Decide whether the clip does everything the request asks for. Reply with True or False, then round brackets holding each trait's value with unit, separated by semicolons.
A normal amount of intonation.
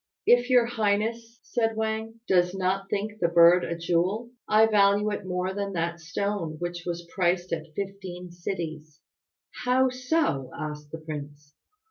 True (4.3 semitones)